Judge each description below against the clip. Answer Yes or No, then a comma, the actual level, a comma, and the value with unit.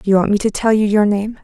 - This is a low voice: No, high, 210 Hz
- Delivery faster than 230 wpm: Yes, fast, 375 wpm